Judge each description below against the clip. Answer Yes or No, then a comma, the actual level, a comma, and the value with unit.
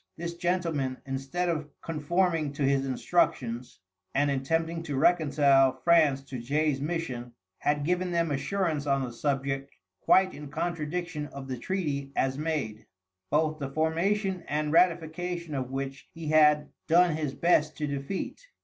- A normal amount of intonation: Yes, average, 3.7 semitones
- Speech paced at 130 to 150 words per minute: Yes, average, 145 wpm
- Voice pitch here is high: No, medium, 150 Hz